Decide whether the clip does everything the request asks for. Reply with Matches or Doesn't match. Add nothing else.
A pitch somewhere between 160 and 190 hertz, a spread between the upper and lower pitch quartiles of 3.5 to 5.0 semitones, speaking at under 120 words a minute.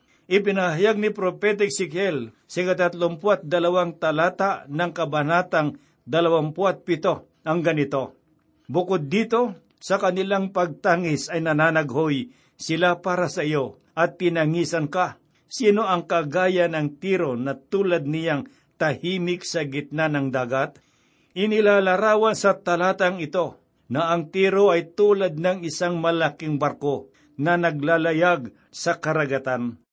Doesn't match